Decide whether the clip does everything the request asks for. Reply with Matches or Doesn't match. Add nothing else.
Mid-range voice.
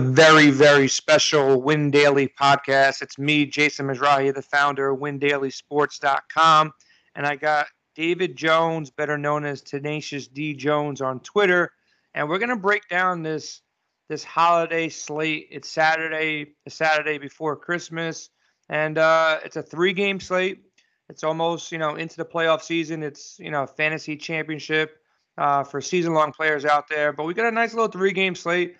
Matches